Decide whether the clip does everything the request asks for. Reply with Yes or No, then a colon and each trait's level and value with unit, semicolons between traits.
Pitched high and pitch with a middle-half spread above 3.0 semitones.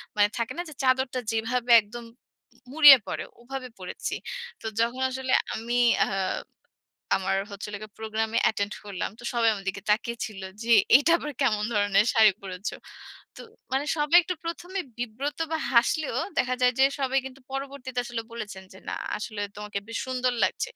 Yes: high, 235 Hz; average, 4.0 semitones